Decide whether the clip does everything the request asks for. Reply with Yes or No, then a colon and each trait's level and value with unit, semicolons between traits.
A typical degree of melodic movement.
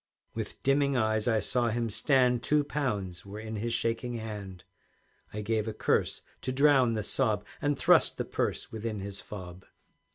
Yes: average, 3.4 semitones